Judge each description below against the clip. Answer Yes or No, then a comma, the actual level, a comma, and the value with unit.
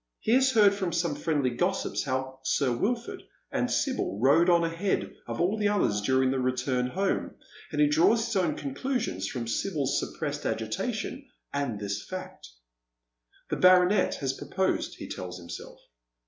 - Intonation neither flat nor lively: No, wide, 7.7 semitones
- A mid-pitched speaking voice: Yes, medium, 165 Hz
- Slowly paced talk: No, average, 160 wpm